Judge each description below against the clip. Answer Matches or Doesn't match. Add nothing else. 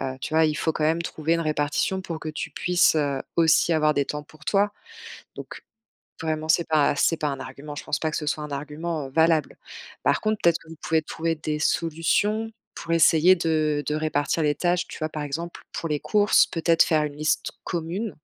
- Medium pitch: Matches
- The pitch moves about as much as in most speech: Doesn't match